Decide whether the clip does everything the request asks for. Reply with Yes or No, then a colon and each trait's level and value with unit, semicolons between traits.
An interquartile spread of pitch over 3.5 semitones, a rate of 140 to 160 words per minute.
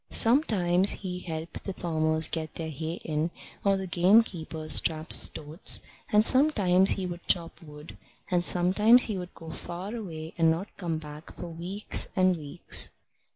No: average, 3.2 semitones; average, 155 wpm